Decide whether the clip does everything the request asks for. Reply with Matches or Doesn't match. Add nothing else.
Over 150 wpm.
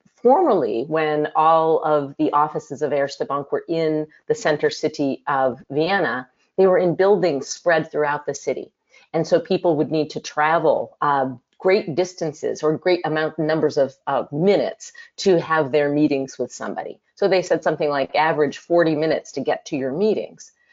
Matches